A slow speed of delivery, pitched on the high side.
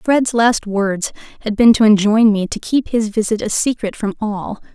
No: average, 200 wpm; high, 215 Hz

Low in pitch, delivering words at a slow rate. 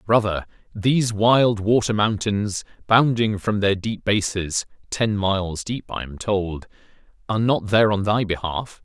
No: low, 105 Hz; average, 150 wpm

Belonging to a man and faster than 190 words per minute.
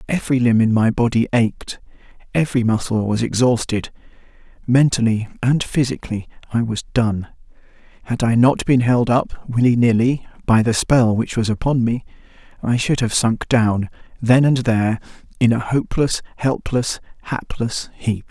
No: male; average, 150 wpm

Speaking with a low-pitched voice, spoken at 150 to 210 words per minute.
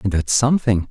Yes: low, 110 Hz; average, 200 wpm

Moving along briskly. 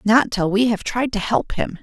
Yes: fast, 265 wpm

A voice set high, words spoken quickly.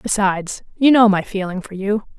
No: high, 200 Hz; average, 195 wpm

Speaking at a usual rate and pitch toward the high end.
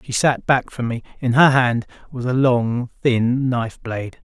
No: average, 195 wpm; low, 125 Hz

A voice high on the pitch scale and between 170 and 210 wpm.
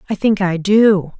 Yes: high, 195 Hz; average, 200 wpm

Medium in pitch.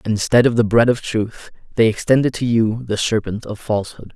No: low, 115 Hz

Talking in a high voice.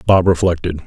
No: very low, 85 Hz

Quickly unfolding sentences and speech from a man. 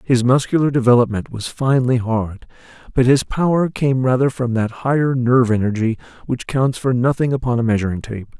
No: average, 170 wpm; male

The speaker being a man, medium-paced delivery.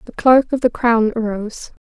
No: female; average, 195 wpm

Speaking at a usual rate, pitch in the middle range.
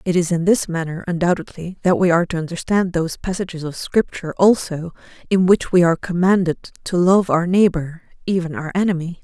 Yes: average, 180 wpm; medium, 175 Hz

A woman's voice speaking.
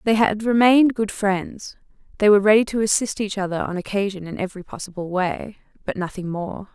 Yes: female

